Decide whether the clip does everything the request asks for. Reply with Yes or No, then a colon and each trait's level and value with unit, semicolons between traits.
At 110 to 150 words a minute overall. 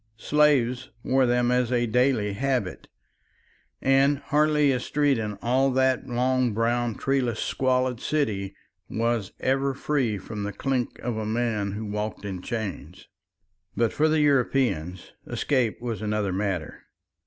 Yes: average, 140 wpm